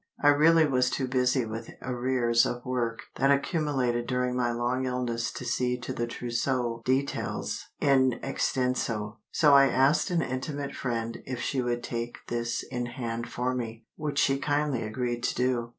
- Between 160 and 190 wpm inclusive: Yes, average, 165 wpm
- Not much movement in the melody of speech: Yes, narrow, 2.2 semitones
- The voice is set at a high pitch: No, low, 125 Hz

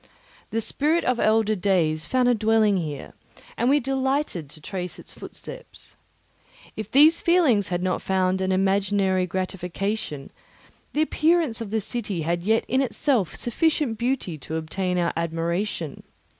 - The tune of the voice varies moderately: No, wide, 5.7 semitones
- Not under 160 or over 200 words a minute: No, average, 145 wpm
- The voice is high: Yes, high, 205 Hz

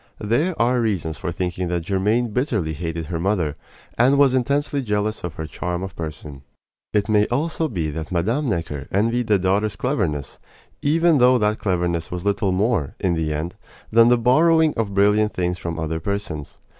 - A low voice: Yes, low, 100 Hz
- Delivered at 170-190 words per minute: Yes, average, 180 wpm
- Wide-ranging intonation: Yes, wide, 6.0 semitones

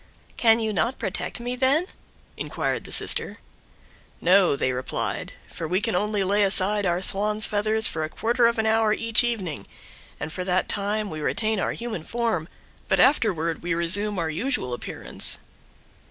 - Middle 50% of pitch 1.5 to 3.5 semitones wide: No, average, 4.3 semitones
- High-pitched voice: Yes, high, 205 Hz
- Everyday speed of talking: Yes, average, 170 wpm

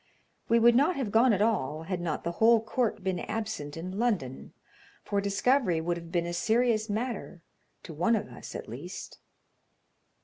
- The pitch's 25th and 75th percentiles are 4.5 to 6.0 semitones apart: Yes, average, 5.1 semitones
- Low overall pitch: No, high, 200 Hz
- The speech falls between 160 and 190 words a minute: Yes, average, 175 wpm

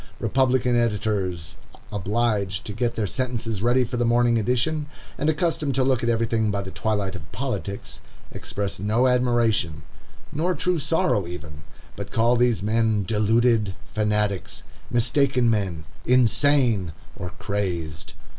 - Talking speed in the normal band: No, slow, 125 wpm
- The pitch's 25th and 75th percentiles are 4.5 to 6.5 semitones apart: No, average, 3.8 semitones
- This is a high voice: No, low, 115 Hz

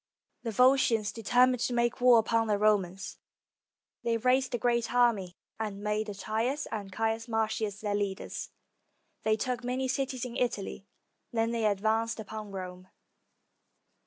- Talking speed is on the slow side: No, average, 145 wpm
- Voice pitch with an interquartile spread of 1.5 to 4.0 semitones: Yes, average, 2.7 semitones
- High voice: Yes, high, 225 Hz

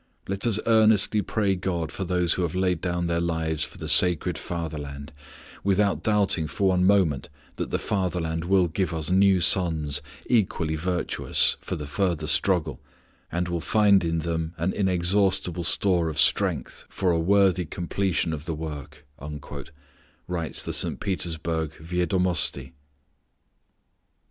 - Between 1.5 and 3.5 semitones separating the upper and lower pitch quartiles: Yes, average, 2.9 semitones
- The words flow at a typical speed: Yes, average, 145 wpm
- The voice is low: Yes, very low, 85 Hz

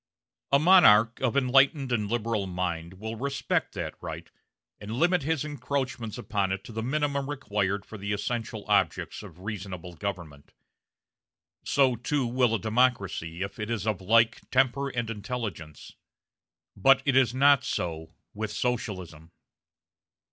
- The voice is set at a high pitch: No, low, 115 Hz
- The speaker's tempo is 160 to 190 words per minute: No, average, 140 wpm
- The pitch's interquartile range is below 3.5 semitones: No, average, 5.0 semitones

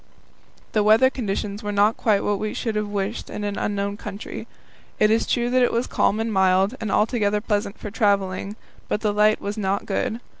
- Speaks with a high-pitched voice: Yes, high, 210 Hz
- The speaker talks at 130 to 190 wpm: No, average, 200 wpm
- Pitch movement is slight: Yes, narrow, 1.6 semitones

